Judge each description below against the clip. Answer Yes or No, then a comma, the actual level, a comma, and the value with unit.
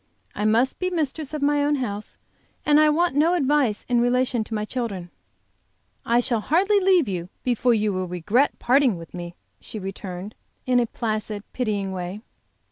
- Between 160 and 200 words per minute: Yes, average, 175 wpm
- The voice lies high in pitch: Yes, high, 240 Hz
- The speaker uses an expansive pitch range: Yes, wide, 6.0 semitones